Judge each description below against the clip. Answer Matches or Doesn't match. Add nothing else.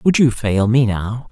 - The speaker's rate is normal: Doesn't match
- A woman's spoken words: Doesn't match